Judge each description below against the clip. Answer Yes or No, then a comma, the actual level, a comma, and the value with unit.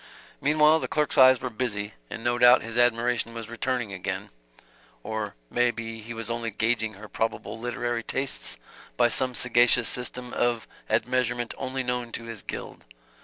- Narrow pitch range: Yes, narrow, 1.7 semitones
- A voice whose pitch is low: Yes, low, 120 Hz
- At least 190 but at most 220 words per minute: No, average, 165 wpm